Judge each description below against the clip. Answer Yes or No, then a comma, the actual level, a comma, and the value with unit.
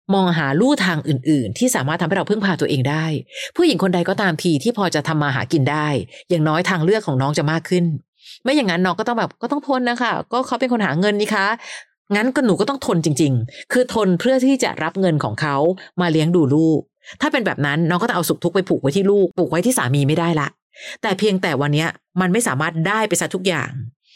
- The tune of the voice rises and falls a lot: Yes, wide, 5.7 semitones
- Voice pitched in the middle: Yes, medium, 180 Hz